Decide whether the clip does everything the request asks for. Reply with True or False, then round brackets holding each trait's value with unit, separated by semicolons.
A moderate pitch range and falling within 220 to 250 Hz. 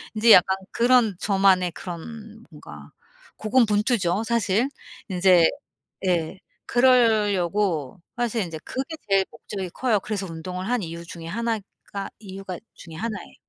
False (4.4 semitones; 195 Hz)